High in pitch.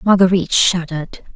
No: medium, 180 Hz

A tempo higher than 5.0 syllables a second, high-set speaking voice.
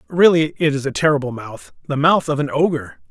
No: 5.6 syllables/s; medium, 140 Hz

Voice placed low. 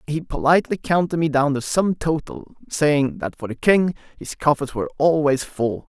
No: medium, 150 Hz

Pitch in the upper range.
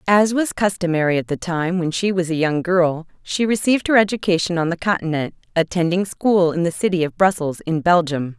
No: medium, 175 Hz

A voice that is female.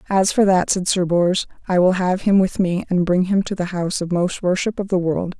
Yes: female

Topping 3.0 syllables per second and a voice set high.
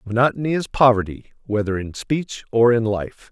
No: 5.0 syllables/s; low, 120 Hz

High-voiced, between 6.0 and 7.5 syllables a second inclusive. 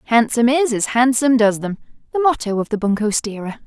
Yes: high, 235 Hz; 6.2 syllables/s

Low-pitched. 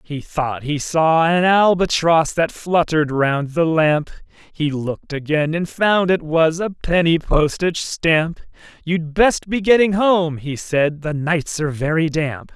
No: medium, 160 Hz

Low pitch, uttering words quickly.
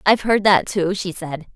No: medium, 185 Hz; fast, 230 wpm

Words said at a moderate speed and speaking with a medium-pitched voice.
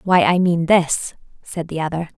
Yes: average, 190 wpm; medium, 170 Hz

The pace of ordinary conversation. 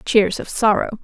Yes: average, 175 wpm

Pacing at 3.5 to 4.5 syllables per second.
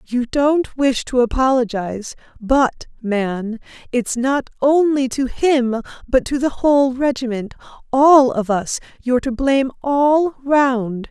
Yes: 3.9 syllables/s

